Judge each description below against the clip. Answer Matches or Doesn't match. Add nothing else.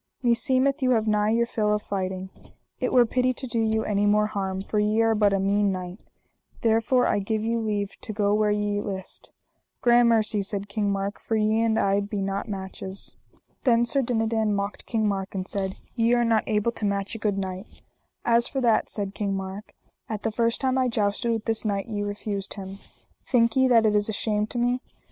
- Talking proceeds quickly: Matches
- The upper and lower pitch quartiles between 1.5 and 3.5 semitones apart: Matches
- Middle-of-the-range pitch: Doesn't match